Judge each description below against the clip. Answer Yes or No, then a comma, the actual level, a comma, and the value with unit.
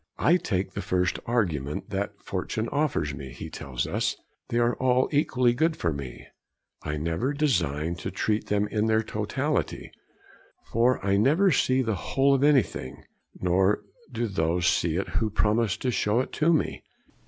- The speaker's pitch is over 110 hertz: No, low, 105 Hz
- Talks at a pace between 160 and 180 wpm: Yes, average, 165 wpm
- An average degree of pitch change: No, wide, 6.6 semitones